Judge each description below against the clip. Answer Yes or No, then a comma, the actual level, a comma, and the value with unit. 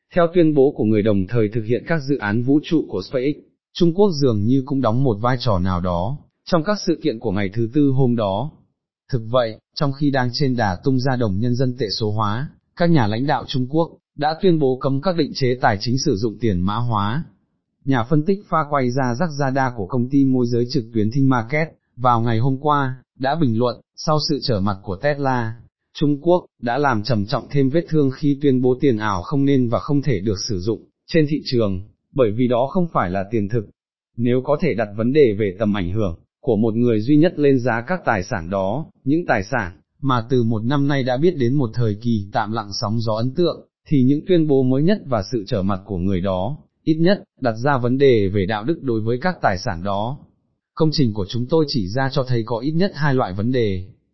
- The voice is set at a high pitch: No, low, 125 Hz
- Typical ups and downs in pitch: Yes, average, 4.6 semitones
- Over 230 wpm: Yes, average, 245 wpm